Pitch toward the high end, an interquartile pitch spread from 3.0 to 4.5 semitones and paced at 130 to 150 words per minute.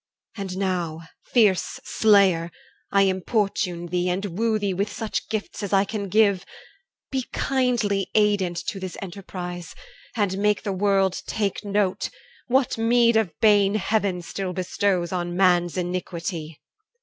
No: high, 195 Hz; narrow, 2.6 semitones; slow, 135 wpm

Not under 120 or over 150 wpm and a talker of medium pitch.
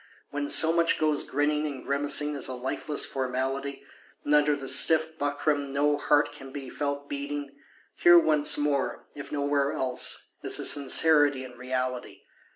No: average, 160 wpm; medium, 145 Hz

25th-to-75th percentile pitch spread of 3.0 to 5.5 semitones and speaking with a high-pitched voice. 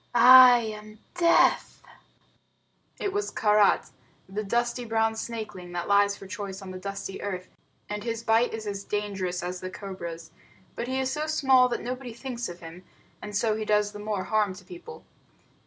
Yes: average, 3.7 semitones; high, 210 Hz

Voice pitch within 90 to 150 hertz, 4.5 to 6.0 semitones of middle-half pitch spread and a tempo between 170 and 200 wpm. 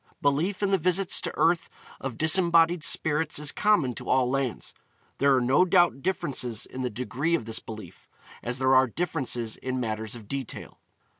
Yes: low, 135 Hz; wide, 5.4 semitones; average, 175 wpm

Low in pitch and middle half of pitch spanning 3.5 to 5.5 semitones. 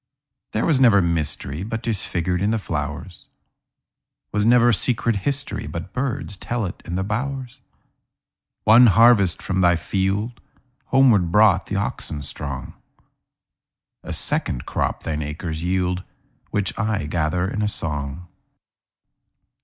Yes: low, 100 Hz; average, 4.8 semitones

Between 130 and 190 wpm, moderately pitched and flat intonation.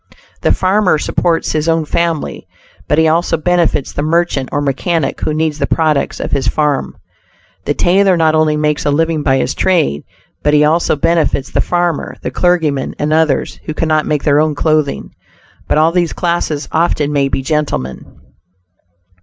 Yes: average, 170 wpm; medium, 155 Hz; narrow, 2.2 semitones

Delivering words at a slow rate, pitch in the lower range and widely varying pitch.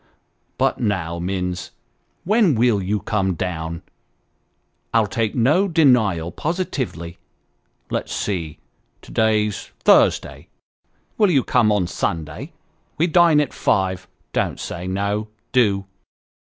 Yes: slow, 110 wpm; low, 105 Hz; wide, 6.1 semitones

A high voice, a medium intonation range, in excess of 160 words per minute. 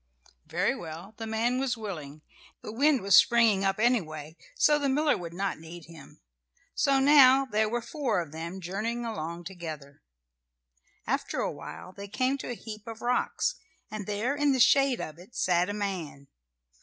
No: high, 210 Hz; wide, 6.3 semitones; average, 170 wpm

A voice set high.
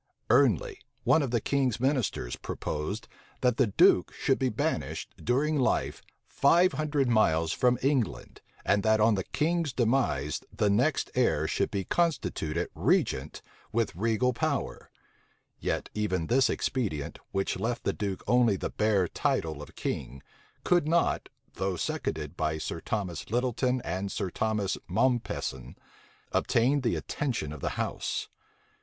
No: low, 110 Hz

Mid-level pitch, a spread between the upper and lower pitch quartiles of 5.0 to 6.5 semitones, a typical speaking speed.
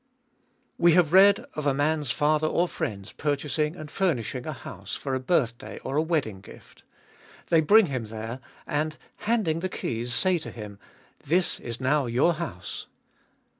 Yes: medium, 150 Hz; wide, 5.5 semitones; average, 170 wpm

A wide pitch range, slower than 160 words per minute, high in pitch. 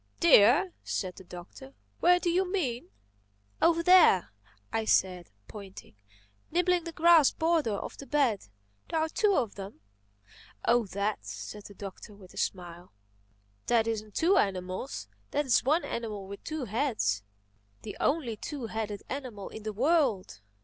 Yes: wide, 8.5 semitones; average, 140 wpm; high, 225 Hz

